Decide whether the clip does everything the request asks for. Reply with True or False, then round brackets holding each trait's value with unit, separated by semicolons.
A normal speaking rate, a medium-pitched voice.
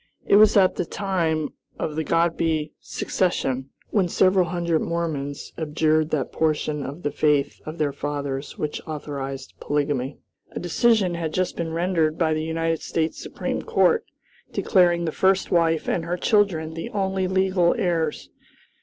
True (155 wpm; 165 Hz)